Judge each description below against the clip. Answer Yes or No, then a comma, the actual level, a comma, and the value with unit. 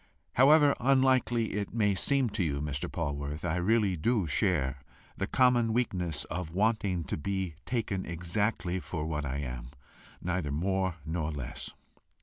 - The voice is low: Yes, very low, 90 Hz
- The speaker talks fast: No, average, 145 wpm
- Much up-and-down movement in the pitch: Yes, wide, 6.2 semitones